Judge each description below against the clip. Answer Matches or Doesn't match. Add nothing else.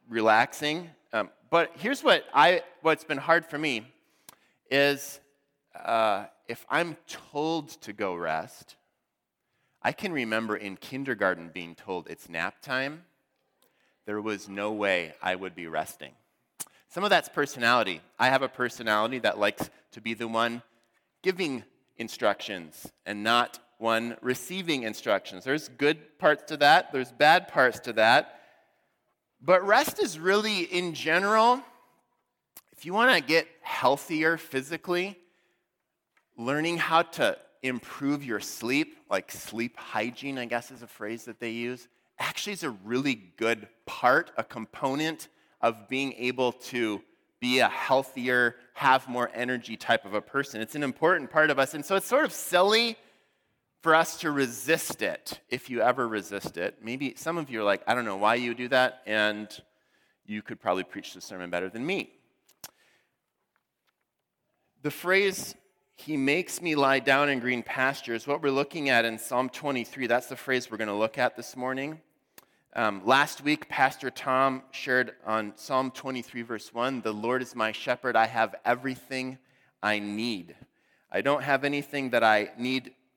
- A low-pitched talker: Matches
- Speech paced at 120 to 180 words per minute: Matches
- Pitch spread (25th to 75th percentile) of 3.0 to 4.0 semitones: Doesn't match